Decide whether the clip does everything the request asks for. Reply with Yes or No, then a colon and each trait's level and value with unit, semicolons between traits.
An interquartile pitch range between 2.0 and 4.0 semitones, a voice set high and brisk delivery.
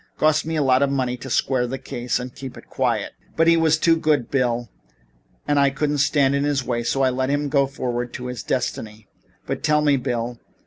No: average, 2.9 semitones; low, 135 Hz; fast, 220 wpm